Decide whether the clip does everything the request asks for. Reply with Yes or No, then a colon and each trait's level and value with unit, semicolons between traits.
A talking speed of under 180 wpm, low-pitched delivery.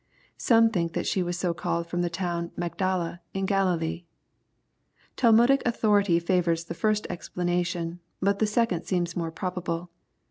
No: average, 155 wpm; medium, 180 Hz